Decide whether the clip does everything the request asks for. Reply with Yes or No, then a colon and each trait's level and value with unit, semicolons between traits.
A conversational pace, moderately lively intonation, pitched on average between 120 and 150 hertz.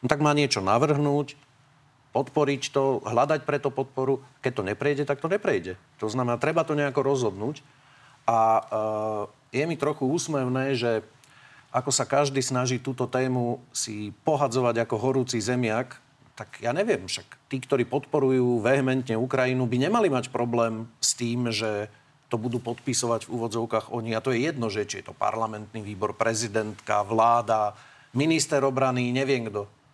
Yes: average, 155 wpm; average, 3.7 semitones; low, 125 Hz